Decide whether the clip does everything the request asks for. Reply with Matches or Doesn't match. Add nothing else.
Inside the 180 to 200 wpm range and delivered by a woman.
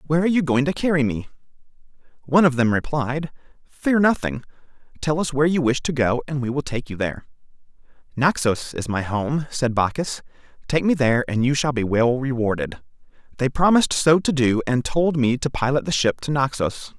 Doesn't match